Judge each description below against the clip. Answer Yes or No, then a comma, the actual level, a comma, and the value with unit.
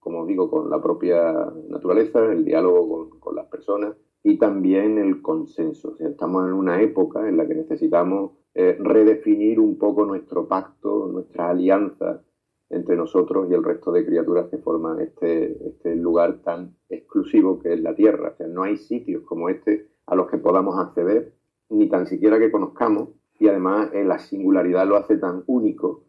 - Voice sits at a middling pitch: No, low, 105 Hz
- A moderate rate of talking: Yes, average, 180 wpm